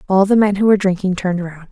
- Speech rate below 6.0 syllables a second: No, 7.2 syllables/s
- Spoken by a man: No, female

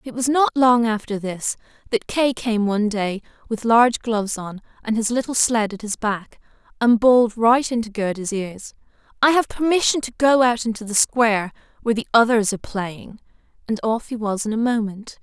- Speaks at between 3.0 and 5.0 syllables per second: No, 5.3 syllables/s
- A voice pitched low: No, high, 225 Hz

